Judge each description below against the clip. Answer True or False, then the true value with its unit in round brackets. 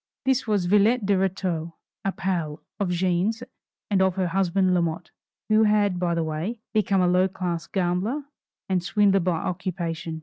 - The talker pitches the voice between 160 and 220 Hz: True (185 Hz)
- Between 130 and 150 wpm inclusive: False (165 wpm)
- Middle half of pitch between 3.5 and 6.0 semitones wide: False (2.7 semitones)